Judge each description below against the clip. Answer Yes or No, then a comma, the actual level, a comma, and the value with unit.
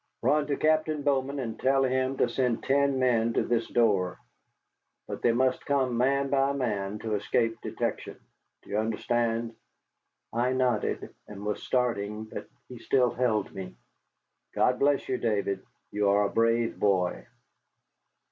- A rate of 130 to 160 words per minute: Yes, average, 150 wpm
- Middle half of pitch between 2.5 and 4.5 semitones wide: Yes, average, 3.6 semitones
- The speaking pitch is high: No, low, 120 Hz